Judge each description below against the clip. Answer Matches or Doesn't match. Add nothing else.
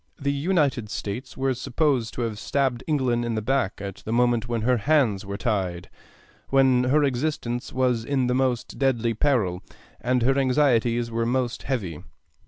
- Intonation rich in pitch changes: Doesn't match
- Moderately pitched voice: Doesn't match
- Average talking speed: Matches